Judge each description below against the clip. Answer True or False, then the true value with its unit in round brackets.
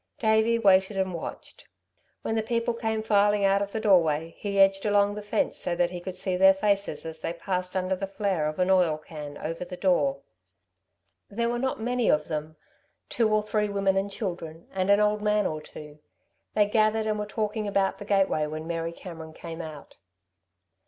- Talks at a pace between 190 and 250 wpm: True (200 wpm)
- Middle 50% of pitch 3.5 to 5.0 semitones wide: True (3.9 semitones)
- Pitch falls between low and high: False (195 Hz)